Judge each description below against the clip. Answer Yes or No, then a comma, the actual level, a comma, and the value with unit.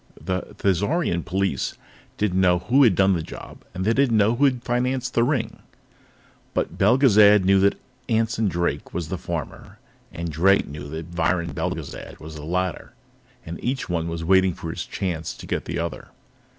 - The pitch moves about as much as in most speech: Yes, average, 5.0 semitones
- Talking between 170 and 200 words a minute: Yes, average, 175 wpm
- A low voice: Yes, very low, 95 Hz